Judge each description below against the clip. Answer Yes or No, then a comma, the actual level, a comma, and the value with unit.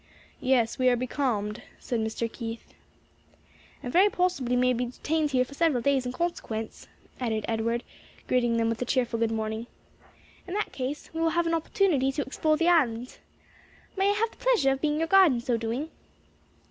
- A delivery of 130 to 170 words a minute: No, average, 185 wpm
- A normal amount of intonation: No, wide, 5.7 semitones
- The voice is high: Yes, very high, 255 Hz